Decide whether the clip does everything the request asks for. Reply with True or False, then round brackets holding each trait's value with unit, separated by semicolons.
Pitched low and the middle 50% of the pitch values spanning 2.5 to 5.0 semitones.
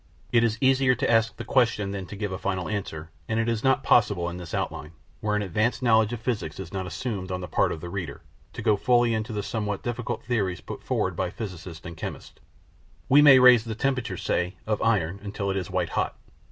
True (105 Hz; 4.1 semitones)